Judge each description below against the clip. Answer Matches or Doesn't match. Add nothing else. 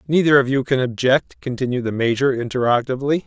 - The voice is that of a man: Matches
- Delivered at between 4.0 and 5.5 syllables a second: Doesn't match